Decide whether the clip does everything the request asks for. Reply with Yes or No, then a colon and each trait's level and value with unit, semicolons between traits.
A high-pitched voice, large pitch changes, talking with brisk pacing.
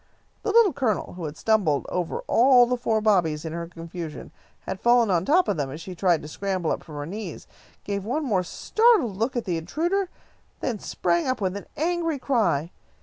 Yes: high, 200 Hz; wide, 6.9 semitones; fast, 210 wpm